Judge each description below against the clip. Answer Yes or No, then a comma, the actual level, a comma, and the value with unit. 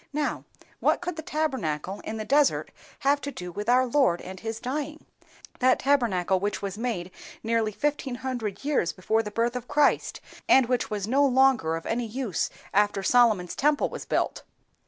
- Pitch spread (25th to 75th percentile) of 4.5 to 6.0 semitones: Yes, average, 5.0 semitones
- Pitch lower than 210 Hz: No, high, 240 Hz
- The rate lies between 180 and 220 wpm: No, average, 170 wpm